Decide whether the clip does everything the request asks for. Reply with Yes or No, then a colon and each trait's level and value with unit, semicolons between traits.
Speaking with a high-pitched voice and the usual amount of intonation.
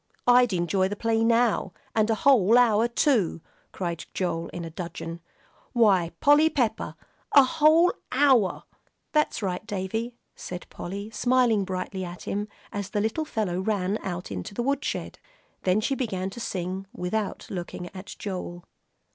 Yes: high, 205 Hz; average, 4.6 semitones